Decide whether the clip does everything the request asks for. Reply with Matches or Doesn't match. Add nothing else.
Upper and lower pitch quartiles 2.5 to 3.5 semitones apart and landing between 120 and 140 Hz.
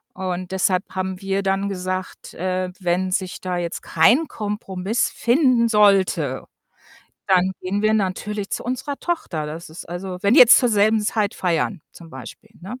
Doesn't match